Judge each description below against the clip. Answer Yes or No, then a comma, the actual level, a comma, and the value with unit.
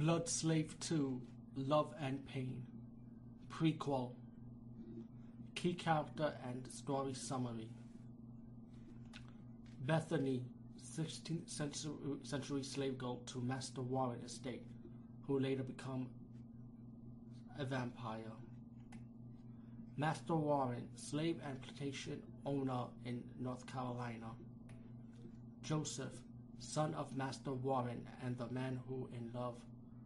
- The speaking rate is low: Yes, slow, 95 wpm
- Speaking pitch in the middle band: No, low, 120 Hz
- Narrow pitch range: Yes, narrow, 2.3 semitones